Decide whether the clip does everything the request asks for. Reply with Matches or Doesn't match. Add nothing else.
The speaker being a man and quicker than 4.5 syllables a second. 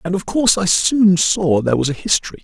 Matches